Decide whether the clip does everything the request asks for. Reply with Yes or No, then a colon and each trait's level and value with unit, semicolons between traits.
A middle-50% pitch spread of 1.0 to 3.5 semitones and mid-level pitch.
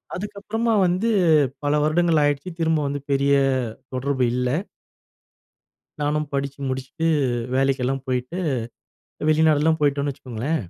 Yes: average, 3.1 semitones; medium, 145 Hz